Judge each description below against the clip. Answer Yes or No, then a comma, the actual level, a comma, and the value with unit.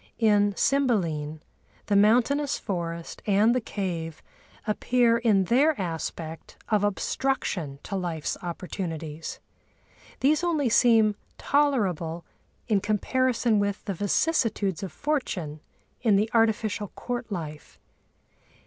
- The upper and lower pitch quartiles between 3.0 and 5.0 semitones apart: No, wide, 5.6 semitones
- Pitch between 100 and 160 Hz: No, high, 205 Hz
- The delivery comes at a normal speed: No, slow, 105 wpm